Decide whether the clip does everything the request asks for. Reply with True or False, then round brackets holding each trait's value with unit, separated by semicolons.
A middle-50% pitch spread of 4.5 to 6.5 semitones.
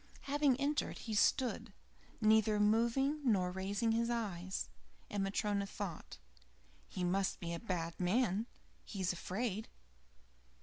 False (3.7 semitones)